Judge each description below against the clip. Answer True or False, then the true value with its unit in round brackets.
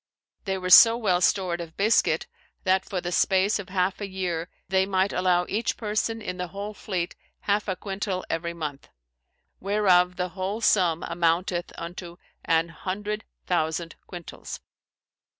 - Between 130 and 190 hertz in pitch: True (185 Hz)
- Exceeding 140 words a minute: True (150 wpm)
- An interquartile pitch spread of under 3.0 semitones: True (2.4 semitones)